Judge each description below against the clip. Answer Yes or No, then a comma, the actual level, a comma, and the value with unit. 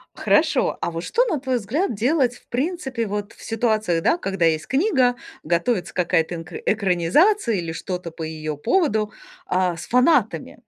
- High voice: Yes, high, 215 Hz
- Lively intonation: Yes, wide, 7.4 semitones